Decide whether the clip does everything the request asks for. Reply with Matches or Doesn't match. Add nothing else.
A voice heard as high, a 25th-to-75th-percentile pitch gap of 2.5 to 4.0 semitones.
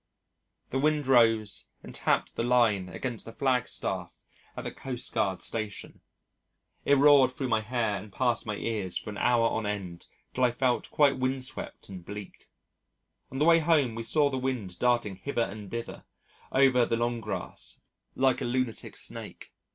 Doesn't match